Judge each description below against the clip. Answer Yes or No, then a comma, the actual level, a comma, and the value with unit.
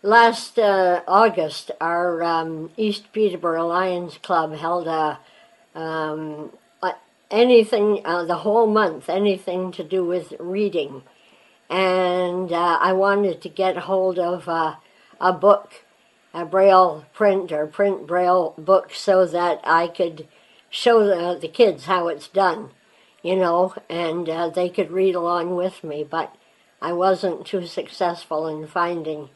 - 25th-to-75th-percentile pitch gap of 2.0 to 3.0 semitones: Yes, narrow, 2.6 semitones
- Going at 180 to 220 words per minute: No, average, 140 wpm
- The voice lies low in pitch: No, medium, 180 Hz